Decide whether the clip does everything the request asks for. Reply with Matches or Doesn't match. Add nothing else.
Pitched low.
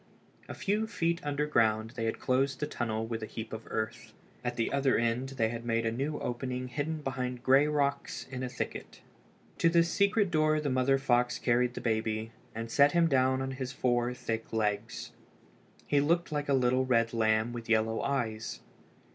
Matches